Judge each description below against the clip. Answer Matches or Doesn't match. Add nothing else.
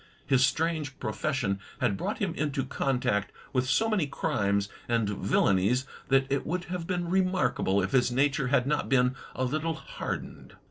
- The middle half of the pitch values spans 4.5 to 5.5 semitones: Matches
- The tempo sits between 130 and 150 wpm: Doesn't match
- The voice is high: Doesn't match